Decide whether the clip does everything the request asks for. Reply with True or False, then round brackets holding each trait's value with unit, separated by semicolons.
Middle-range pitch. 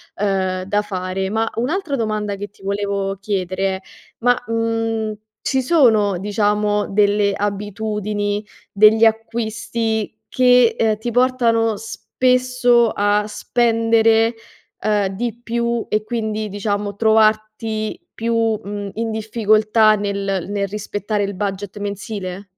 False (215 Hz)